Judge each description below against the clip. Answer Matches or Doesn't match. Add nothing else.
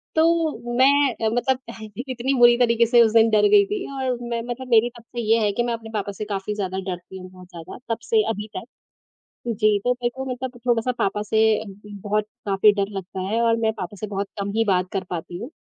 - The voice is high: Matches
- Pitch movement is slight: Doesn't match